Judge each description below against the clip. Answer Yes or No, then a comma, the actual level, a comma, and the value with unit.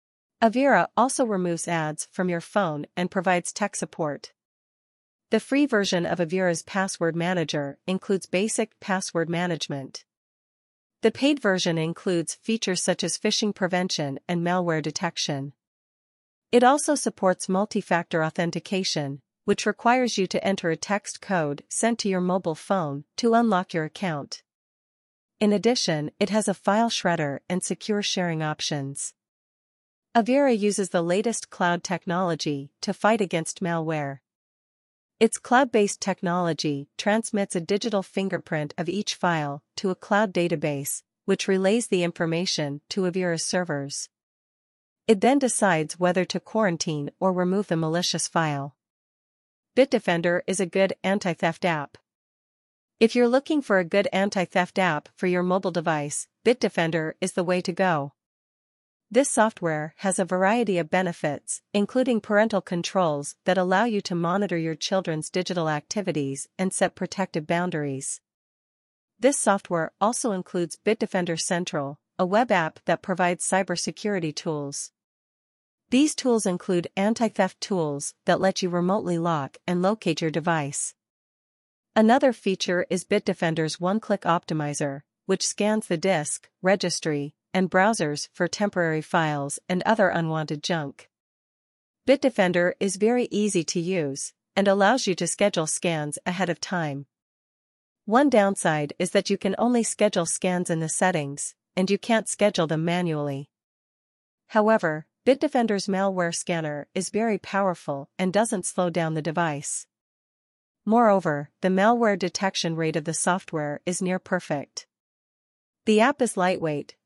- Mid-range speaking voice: Yes, medium, 180 Hz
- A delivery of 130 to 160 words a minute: Yes, slow, 135 wpm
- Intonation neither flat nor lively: Yes, average, 3.7 semitones